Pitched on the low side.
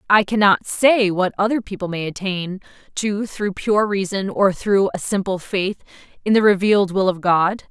No: high, 195 Hz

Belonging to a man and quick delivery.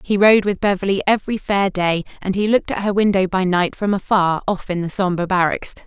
No: female; fast, 225 wpm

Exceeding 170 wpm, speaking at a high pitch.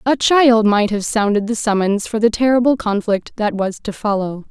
Yes: average, 200 wpm; high, 220 Hz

